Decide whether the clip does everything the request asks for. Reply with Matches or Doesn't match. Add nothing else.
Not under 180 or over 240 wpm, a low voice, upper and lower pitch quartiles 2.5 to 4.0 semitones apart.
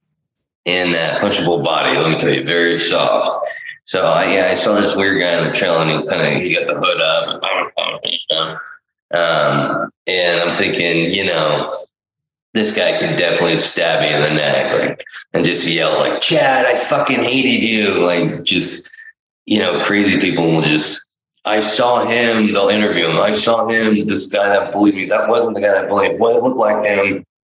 Doesn't match